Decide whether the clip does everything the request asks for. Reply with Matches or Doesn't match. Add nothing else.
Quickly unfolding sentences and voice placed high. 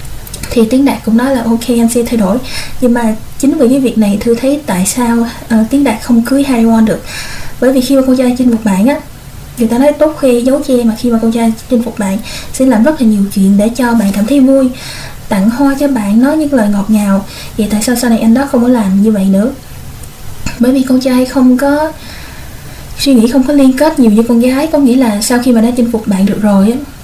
Matches